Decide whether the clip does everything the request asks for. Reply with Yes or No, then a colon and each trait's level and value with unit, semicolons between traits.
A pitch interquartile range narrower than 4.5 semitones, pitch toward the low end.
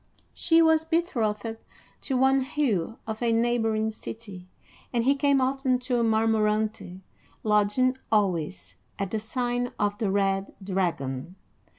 No: average, 4.0 semitones; high, 225 Hz